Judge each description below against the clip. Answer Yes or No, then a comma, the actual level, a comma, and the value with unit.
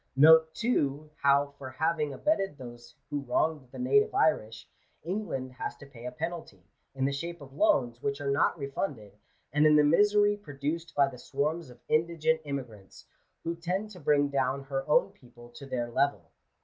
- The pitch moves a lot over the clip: No, average, 3.8 semitones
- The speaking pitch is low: No, medium, 145 Hz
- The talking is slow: No, average, 175 wpm